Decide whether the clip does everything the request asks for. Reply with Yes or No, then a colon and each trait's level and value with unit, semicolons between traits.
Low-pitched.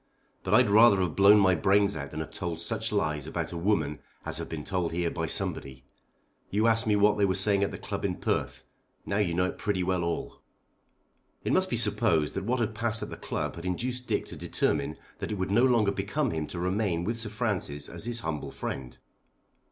Yes: low, 100 Hz